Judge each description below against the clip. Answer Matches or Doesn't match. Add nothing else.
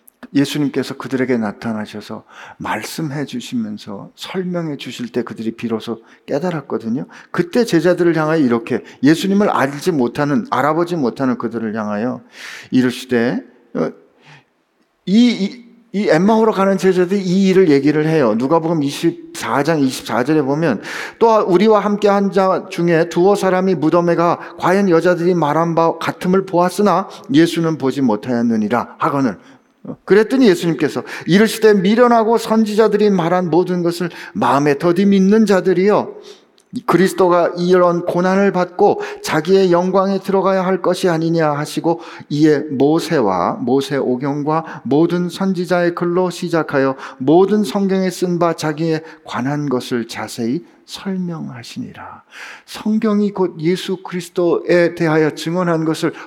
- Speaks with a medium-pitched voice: Matches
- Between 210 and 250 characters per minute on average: Doesn't match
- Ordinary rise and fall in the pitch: Matches